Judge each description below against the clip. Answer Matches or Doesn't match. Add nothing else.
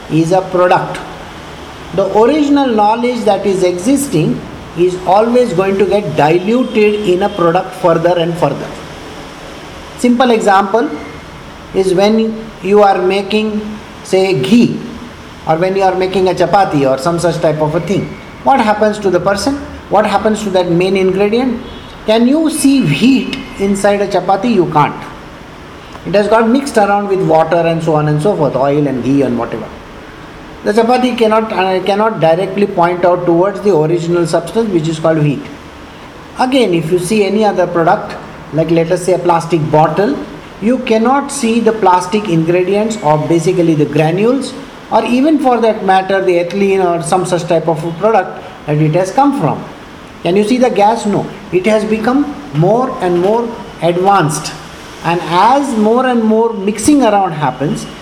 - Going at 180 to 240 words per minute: Doesn't match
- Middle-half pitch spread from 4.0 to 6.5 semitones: Matches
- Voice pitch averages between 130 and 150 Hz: Doesn't match